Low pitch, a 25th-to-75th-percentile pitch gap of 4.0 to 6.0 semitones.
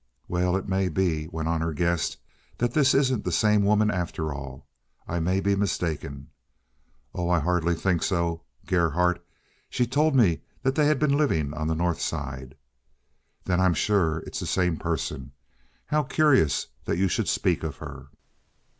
Yes: very low, 90 Hz; average, 4.3 semitones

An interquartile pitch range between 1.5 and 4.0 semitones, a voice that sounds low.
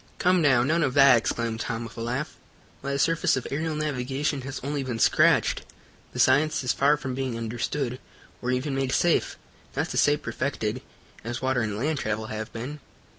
Yes: average, 3.6 semitones; low, 130 Hz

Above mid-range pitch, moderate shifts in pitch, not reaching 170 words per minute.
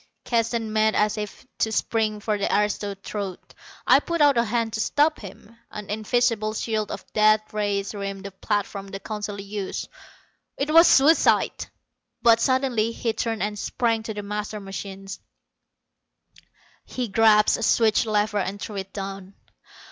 No: high, 215 Hz; narrow, 2.0 semitones; average, 155 wpm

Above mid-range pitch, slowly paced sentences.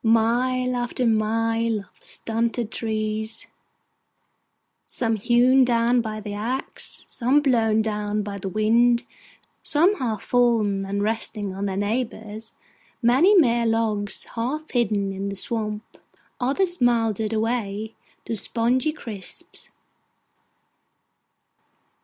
Yes: high, 225 Hz; slow, 110 wpm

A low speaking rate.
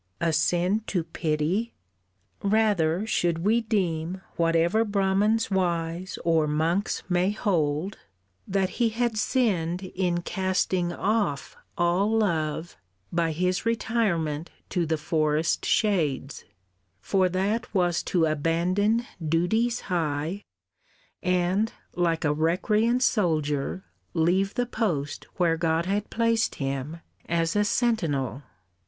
Yes: slow, 110 wpm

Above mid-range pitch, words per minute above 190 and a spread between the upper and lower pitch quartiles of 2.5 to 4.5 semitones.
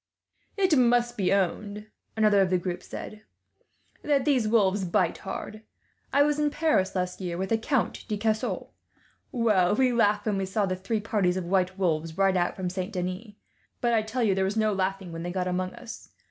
Yes: high, 200 Hz; average, 200 wpm; average, 3.5 semitones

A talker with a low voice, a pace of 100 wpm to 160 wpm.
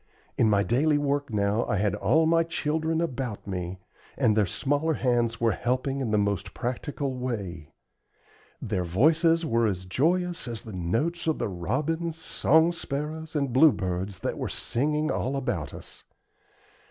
Yes: low, 130 Hz; average, 155 wpm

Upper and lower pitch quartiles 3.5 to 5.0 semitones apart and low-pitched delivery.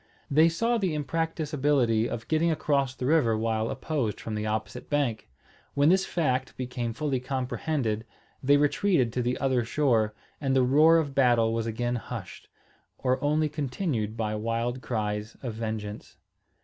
Yes: average, 4.7 semitones; low, 130 Hz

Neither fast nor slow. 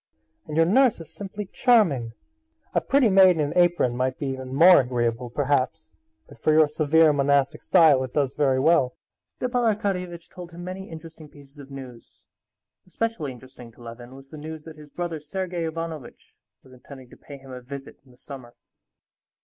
Yes: average, 180 wpm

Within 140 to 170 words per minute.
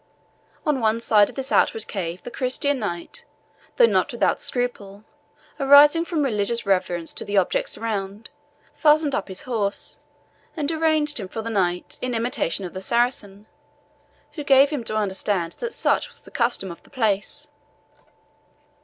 Yes: average, 160 wpm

